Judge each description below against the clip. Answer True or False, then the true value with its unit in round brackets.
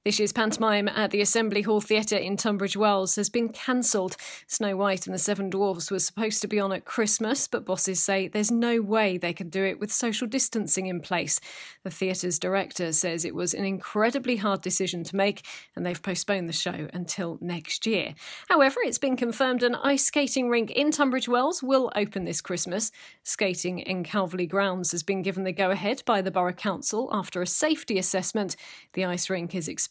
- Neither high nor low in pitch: False (200 Hz)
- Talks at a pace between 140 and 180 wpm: False (200 wpm)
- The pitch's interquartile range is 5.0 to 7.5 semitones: False (3.3 semitones)